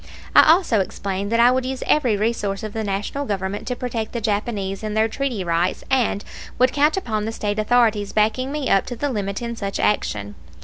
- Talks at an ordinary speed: No, fast, 210 wpm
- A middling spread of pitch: Yes, average, 3.6 semitones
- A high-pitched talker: Yes, high, 220 Hz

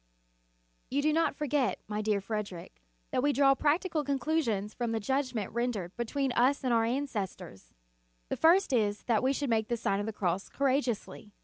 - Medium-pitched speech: No, high, 240 Hz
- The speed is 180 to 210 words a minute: Yes, average, 185 wpm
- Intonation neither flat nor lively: Yes, average, 5.0 semitones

